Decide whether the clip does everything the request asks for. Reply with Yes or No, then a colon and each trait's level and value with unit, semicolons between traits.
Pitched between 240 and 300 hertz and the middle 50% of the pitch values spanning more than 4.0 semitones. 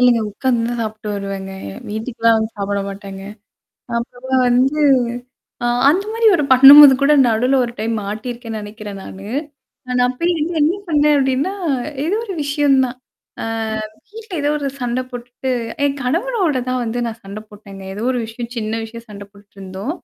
Yes: high, 245 Hz; average, 4.6 semitones